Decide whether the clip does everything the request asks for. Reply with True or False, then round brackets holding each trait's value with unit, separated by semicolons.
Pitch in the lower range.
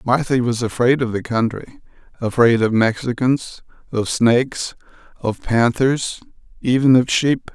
True (120 Hz)